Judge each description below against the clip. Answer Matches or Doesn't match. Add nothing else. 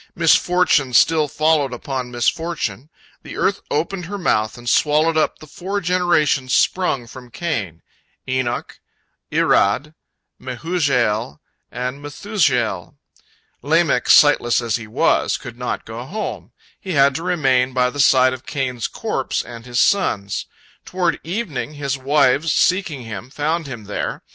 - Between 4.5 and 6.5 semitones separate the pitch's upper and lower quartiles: Matches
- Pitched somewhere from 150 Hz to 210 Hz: Doesn't match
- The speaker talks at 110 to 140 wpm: Matches